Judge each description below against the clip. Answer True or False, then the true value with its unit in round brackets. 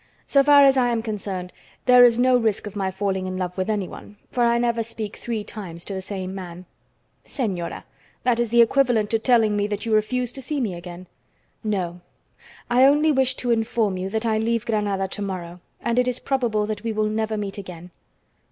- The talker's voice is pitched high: True (215 Hz)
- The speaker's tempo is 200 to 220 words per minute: True (205 wpm)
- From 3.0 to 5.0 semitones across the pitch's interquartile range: True (3.8 semitones)